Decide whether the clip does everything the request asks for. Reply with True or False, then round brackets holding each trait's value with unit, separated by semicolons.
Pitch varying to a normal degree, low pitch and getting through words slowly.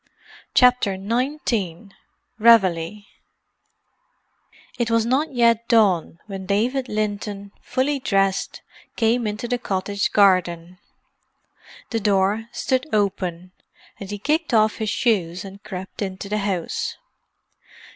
False (3.4 semitones; 205 Hz; 110 wpm)